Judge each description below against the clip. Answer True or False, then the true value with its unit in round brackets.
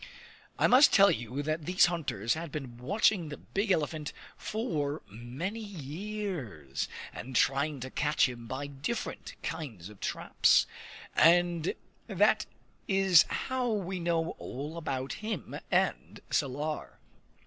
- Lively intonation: True (6.0 semitones)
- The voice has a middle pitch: True (155 Hz)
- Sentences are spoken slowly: True (130 wpm)